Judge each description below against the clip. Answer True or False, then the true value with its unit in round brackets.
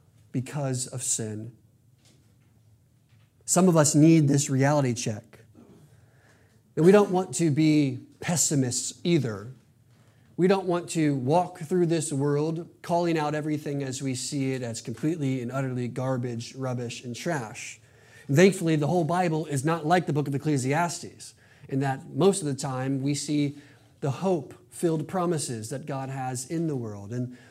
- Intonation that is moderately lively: True (4.4 semitones)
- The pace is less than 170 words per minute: True (155 wpm)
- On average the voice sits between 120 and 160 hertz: True (135 Hz)